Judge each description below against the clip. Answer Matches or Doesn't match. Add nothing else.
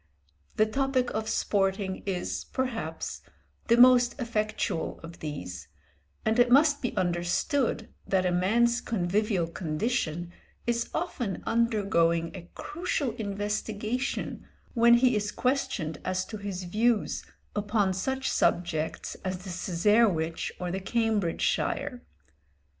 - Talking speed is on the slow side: Matches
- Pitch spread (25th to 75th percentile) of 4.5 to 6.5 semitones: Matches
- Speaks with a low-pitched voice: Doesn't match